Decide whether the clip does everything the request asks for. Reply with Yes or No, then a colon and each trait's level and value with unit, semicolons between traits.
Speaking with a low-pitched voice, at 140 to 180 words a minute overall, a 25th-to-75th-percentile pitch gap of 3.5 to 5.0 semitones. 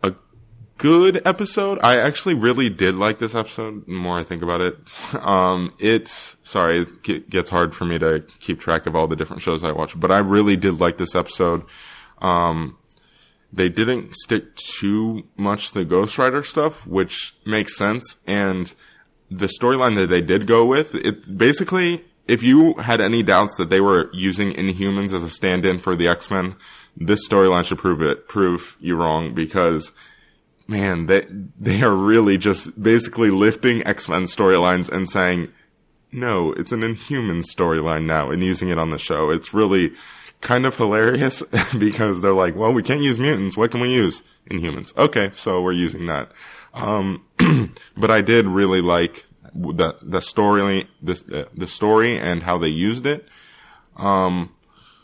Yes: low, 100 Hz; average, 170 wpm; average, 4.0 semitones